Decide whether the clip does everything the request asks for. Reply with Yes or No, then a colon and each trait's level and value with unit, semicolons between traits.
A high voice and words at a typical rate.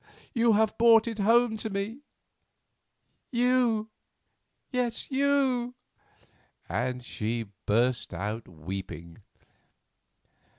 No: high, 220 Hz; slow, 85 wpm